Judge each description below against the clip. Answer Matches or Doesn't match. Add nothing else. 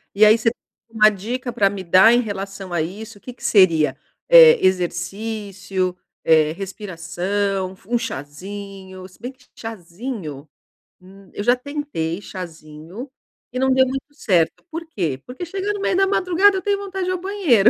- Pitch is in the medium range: Doesn't match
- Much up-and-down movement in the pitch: Matches